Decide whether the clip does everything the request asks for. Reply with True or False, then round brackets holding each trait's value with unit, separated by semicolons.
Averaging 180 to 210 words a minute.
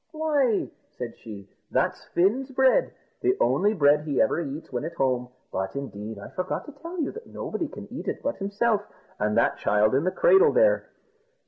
True (190 wpm)